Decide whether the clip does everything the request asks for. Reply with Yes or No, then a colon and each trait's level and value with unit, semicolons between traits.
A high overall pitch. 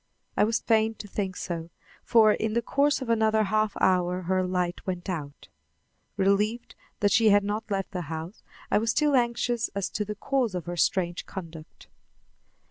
Yes: high, 205 Hz